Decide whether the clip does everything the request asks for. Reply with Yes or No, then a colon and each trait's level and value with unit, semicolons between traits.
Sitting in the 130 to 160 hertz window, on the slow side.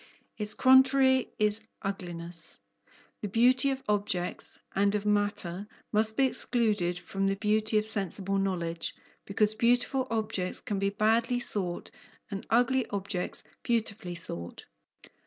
No: high, 210 Hz; slow, 125 wpm